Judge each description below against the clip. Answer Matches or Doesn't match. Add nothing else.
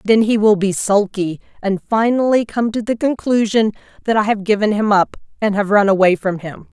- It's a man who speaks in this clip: Doesn't match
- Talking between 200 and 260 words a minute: Matches